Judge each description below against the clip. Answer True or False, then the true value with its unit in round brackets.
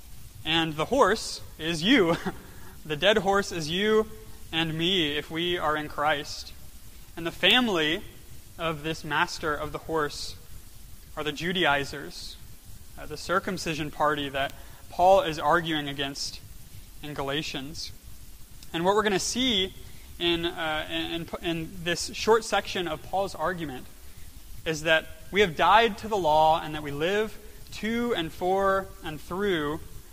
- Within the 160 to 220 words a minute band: False (145 wpm)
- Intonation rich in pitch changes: False (3.9 semitones)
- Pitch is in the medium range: True (160 Hz)